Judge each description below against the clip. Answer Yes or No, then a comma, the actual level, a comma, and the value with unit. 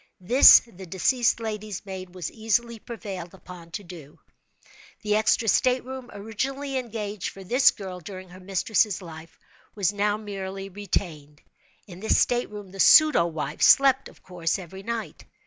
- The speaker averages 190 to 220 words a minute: No, average, 155 wpm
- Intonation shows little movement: No, average, 3.7 semitones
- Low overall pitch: No, high, 200 Hz